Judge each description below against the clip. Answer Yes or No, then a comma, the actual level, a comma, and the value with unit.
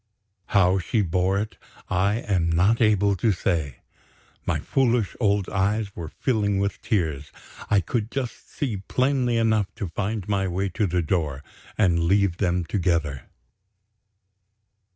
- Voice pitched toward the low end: Yes, low, 100 Hz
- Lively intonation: No, average, 3.4 semitones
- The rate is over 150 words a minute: No, average, 140 wpm